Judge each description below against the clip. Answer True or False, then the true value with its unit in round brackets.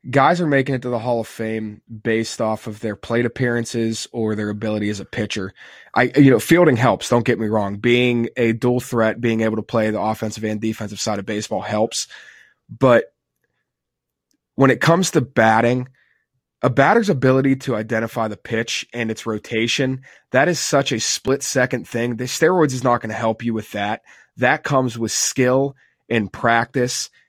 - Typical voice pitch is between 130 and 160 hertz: False (115 Hz)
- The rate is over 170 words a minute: True (185 wpm)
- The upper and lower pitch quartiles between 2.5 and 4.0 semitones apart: True (2.8 semitones)